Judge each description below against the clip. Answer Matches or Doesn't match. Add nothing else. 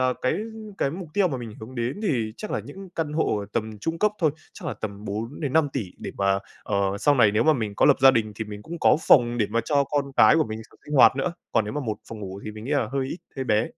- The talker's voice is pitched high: Doesn't match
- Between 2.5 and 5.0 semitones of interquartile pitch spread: Doesn't match